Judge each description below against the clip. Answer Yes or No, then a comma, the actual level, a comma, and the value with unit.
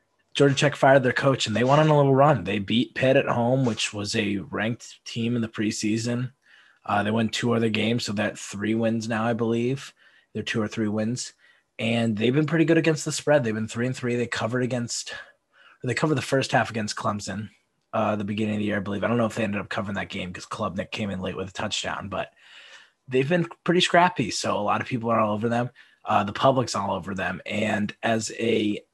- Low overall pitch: Yes, low, 115 Hz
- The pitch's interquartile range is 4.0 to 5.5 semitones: No, average, 3.4 semitones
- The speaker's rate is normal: No, fast, 240 wpm